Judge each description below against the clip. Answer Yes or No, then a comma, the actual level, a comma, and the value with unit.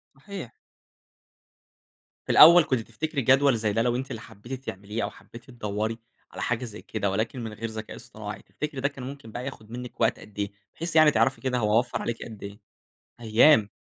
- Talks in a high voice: No, low, 120 Hz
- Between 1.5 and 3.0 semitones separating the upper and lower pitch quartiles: No, average, 3.7 semitones